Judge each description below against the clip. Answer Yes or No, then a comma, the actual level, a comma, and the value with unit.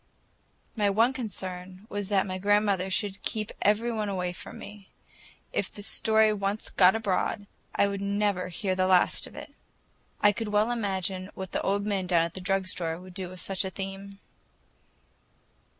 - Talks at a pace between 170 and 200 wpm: Yes, average, 175 wpm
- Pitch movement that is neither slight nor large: No, narrow, 1.9 semitones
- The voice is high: Yes, high, 195 Hz